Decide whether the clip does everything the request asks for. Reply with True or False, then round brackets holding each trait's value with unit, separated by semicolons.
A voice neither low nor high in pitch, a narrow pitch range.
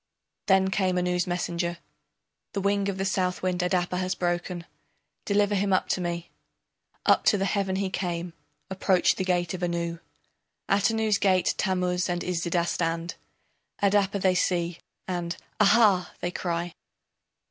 True (180 Hz; 1.8 semitones)